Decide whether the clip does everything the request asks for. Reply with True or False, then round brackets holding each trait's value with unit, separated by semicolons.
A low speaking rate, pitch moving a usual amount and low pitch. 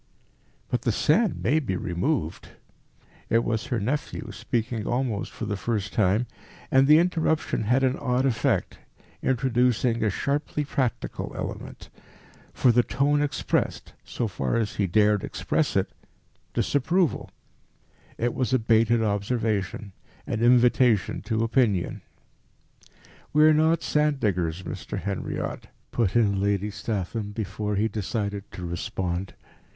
True (130 wpm; 4.3 semitones; 115 Hz)